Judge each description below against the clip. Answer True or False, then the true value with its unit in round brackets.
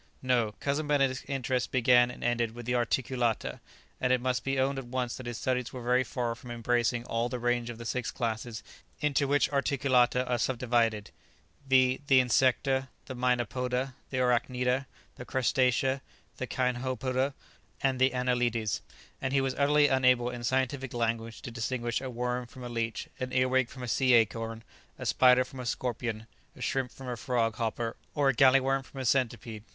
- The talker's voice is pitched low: True (125 Hz)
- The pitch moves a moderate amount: False (1.6 semitones)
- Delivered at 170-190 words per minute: True (180 wpm)